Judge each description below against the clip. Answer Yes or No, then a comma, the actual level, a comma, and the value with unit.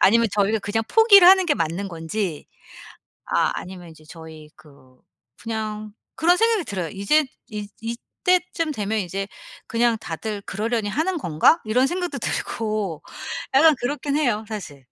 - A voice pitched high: Yes, high, 215 Hz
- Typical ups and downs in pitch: No, wide, 7.5 semitones